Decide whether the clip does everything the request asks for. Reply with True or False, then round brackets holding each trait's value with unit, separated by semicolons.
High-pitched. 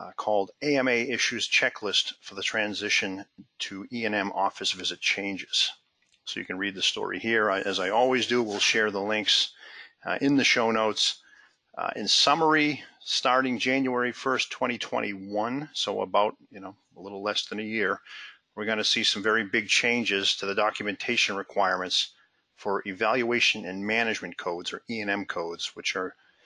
False (105 Hz)